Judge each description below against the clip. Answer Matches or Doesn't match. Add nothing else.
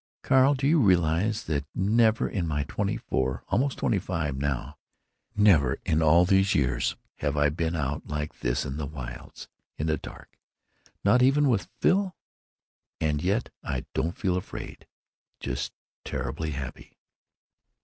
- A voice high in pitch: Doesn't match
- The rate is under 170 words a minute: Matches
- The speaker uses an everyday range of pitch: Doesn't match